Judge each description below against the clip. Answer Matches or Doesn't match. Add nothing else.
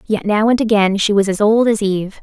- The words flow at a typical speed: Doesn't match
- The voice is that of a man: Doesn't match